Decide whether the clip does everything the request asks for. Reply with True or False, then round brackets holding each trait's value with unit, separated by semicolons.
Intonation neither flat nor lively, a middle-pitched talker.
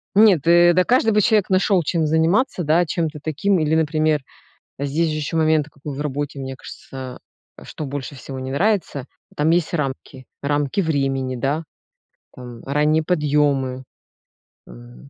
True (3.6 semitones; 150 Hz)